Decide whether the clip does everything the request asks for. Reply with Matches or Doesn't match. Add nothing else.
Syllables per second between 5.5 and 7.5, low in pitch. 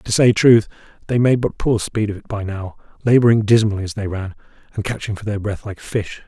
Matches